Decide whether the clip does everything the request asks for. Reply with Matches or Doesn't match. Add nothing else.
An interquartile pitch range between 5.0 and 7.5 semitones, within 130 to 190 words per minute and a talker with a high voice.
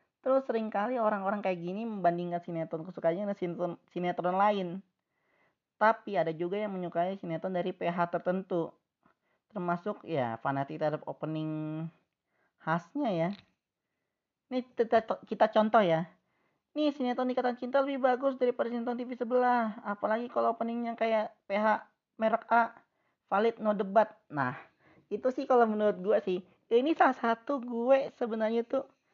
Matches